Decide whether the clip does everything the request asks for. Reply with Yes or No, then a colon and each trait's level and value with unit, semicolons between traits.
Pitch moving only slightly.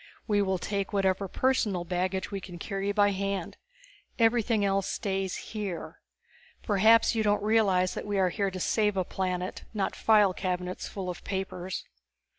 Yes: narrow, 1.9 semitones